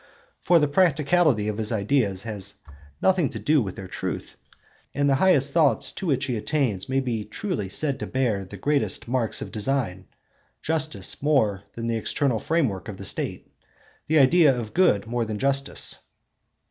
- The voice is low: Yes, low, 130 Hz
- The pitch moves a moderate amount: No, wide, 5.7 semitones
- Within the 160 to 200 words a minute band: Yes, average, 170 wpm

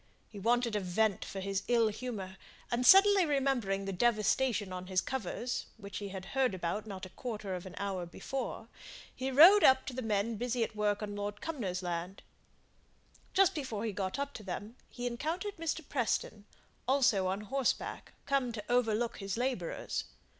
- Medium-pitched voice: No, high, 220 Hz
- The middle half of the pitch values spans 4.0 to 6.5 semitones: Yes, average, 4.7 semitones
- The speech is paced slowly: No, average, 175 wpm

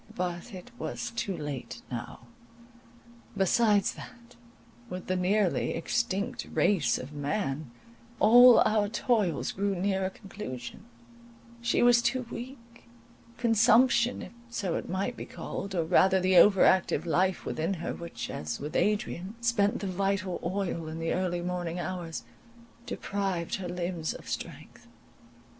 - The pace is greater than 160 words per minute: No, average, 140 wpm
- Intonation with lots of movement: No, average, 3.9 semitones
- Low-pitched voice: No, high, 190 Hz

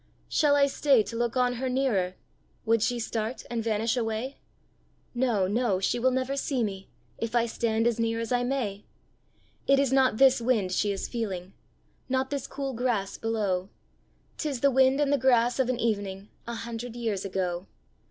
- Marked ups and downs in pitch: No, average, 3.4 semitones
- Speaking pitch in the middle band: No, high, 235 Hz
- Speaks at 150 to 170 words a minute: No, average, 180 wpm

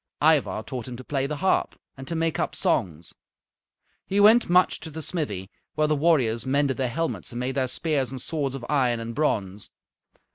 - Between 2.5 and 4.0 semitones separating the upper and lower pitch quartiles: No, average, 4.7 semitones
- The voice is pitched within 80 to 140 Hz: Yes, low, 135 Hz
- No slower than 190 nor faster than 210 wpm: Yes, average, 195 wpm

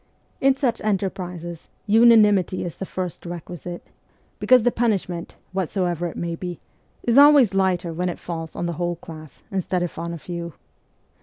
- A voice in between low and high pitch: Yes, medium, 180 Hz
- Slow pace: No, average, 160 wpm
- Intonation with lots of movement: No, average, 3.2 semitones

